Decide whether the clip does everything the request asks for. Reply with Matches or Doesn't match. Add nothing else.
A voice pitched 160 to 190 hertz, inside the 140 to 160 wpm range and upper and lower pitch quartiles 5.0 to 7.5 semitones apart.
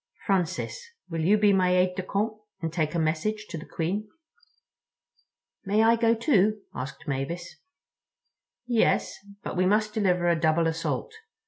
Doesn't match